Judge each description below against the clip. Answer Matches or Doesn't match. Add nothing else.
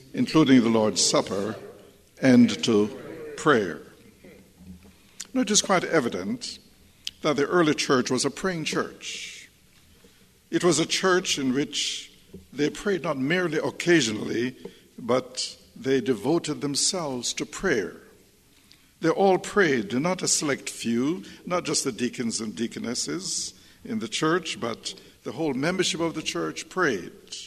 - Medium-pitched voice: Matches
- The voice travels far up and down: Matches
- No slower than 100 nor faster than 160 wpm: Matches